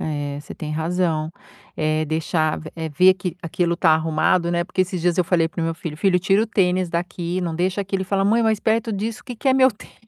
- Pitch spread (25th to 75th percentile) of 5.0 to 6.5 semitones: No, average, 3.2 semitones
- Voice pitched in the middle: Yes, medium, 175 Hz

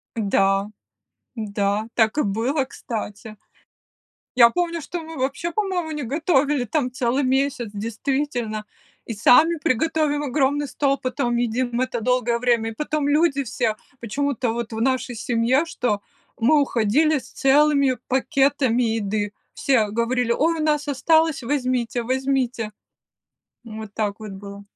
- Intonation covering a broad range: No, average, 4.3 semitones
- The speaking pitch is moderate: No, very high, 255 Hz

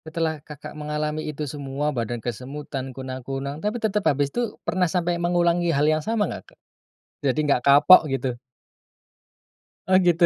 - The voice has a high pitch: No, medium, 150 Hz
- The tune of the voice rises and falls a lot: No, average, 4.1 semitones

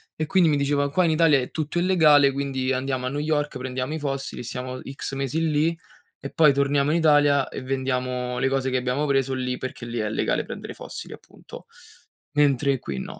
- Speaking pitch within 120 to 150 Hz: Yes, medium, 140 Hz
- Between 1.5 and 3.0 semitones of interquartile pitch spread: Yes, narrow, 2.5 semitones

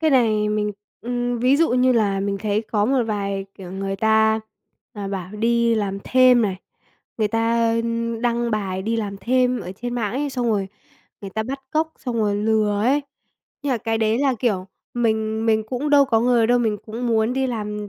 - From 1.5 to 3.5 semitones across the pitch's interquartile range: Yes, average, 2.7 semitones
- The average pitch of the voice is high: Yes, high, 225 Hz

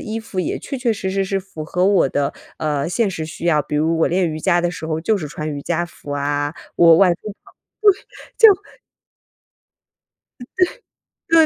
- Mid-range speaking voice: Yes, medium, 170 Hz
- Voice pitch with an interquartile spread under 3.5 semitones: No, average, 4.0 semitones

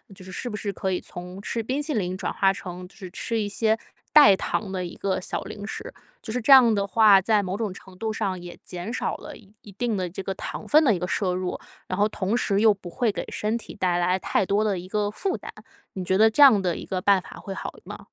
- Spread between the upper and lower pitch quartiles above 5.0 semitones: No, average, 2.9 semitones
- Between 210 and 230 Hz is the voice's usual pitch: No, high, 200 Hz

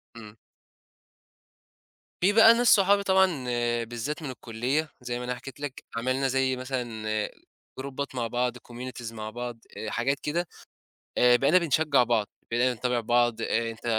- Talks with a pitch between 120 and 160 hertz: Yes, low, 125 Hz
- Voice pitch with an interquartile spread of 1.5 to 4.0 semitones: Yes, average, 3.3 semitones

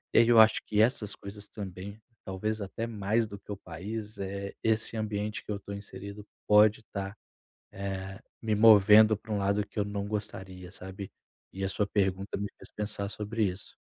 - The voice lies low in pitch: Yes, low, 105 Hz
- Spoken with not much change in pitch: Yes, narrow, 1.6 semitones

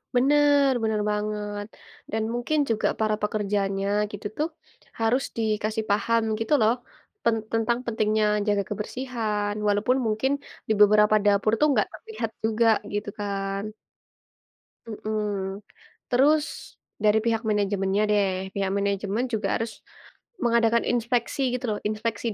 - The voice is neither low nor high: No, high, 215 Hz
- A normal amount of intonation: No, narrow, 2.1 semitones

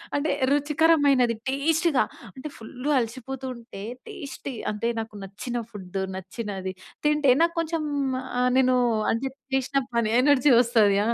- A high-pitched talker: Yes, very high, 255 Hz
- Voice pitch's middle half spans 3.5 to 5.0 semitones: Yes, average, 4.2 semitones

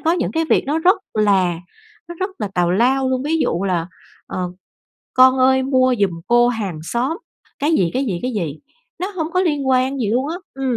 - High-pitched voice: Yes, very high, 255 Hz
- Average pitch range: No, wide, 6.4 semitones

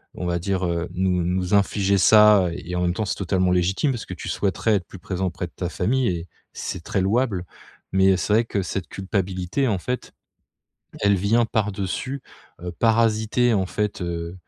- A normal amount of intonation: Yes, average, 3.1 semitones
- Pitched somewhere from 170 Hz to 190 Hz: No, very low, 95 Hz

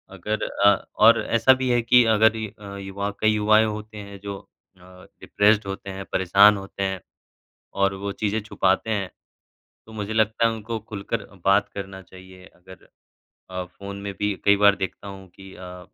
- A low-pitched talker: Yes, low, 100 Hz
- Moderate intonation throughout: No, narrow, 1.9 semitones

